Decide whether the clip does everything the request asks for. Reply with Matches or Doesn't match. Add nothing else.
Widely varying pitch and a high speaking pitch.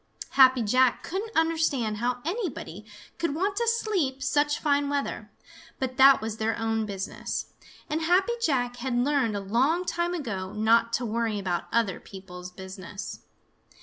Matches